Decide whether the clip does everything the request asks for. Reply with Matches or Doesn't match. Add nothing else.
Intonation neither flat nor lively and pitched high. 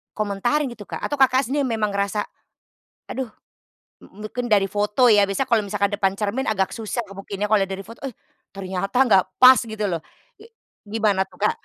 Matches